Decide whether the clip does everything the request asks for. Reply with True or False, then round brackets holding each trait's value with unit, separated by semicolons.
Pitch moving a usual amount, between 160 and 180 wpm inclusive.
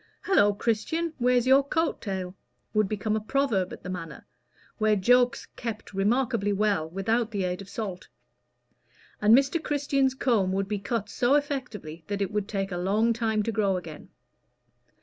True (4.1 semitones; 170 wpm)